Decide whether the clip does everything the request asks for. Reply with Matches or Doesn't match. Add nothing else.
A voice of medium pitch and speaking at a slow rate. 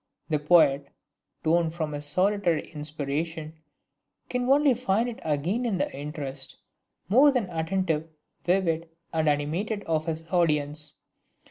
Matches